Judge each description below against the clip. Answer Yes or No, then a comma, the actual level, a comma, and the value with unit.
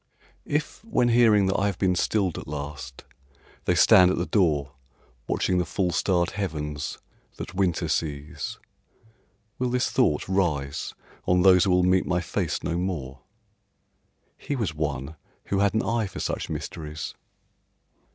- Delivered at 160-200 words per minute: No, average, 150 wpm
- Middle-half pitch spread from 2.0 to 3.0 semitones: No, average, 4.6 semitones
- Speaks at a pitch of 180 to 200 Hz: No, very low, 90 Hz